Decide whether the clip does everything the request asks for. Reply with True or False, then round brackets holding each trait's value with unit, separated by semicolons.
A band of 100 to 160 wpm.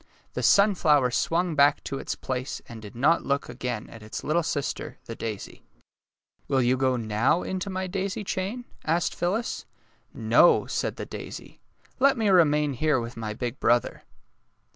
False (180 wpm)